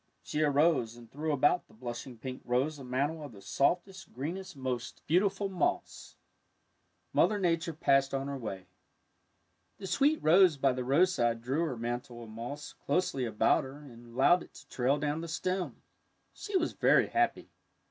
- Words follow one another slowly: No, average, 170 wpm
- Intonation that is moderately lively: No, wide, 5.7 semitones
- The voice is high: No, medium, 140 Hz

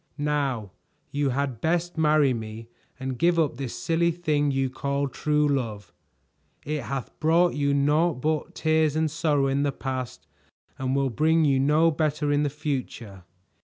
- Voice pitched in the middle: Yes, medium, 145 Hz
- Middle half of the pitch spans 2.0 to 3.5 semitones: Yes, average, 2.9 semitones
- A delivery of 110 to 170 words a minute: Yes, average, 165 wpm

